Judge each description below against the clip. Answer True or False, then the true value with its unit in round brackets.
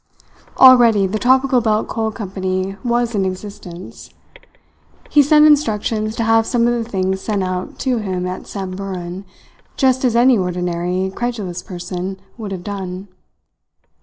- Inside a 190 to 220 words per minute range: False (140 wpm)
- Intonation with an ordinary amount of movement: True (4.2 semitones)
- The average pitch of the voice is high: True (205 Hz)